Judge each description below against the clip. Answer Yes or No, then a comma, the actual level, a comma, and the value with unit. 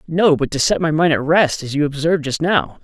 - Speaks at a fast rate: Yes, fast, 275 wpm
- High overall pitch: No, medium, 160 Hz